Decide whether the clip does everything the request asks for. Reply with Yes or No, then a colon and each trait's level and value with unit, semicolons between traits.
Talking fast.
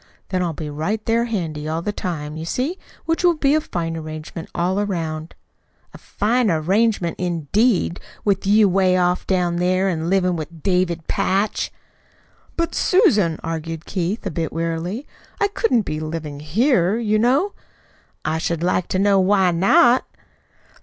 No: average, 160 wpm